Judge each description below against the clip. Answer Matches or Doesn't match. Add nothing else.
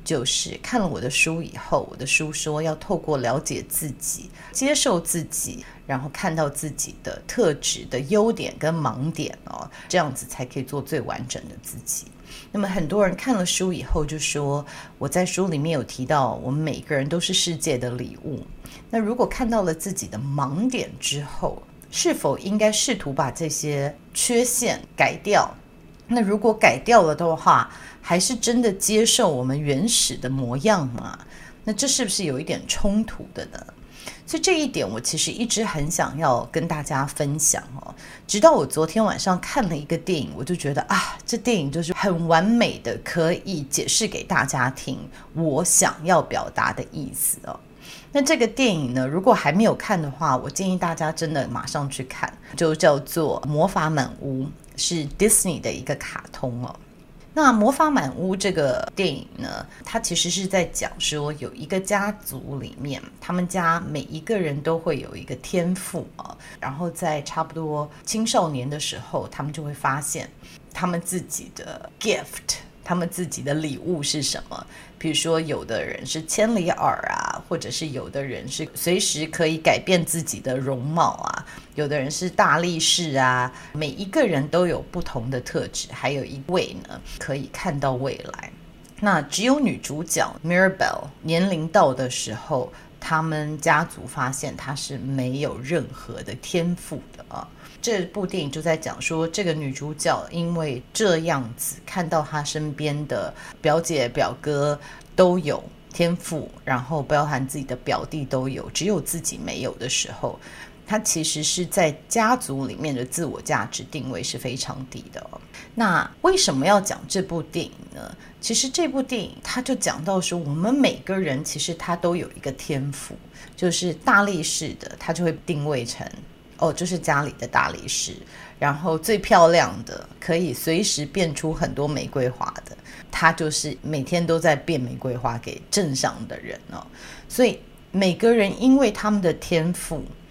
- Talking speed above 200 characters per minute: Matches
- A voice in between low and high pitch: Matches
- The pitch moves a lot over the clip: Doesn't match